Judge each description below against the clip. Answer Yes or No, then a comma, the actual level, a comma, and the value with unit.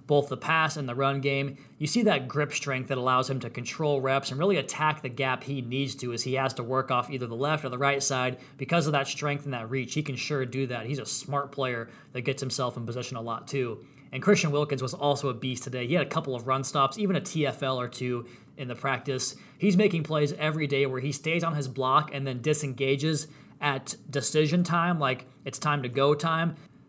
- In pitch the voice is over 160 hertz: No, medium, 140 Hz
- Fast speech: Yes, fast, 245 wpm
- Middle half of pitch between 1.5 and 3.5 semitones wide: Yes, narrow, 2.4 semitones